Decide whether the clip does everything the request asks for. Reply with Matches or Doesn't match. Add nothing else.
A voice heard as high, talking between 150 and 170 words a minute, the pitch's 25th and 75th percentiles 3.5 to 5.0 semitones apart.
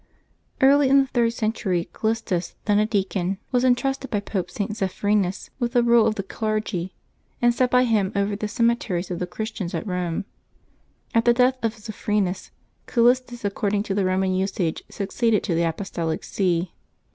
Doesn't match